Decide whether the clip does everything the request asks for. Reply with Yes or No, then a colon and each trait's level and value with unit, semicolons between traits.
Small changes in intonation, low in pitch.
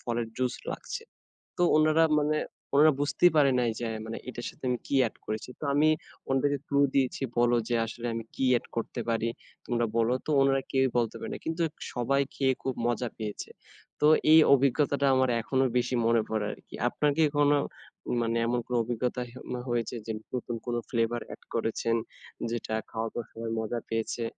No: average, 3.1 semitones; low, 120 Hz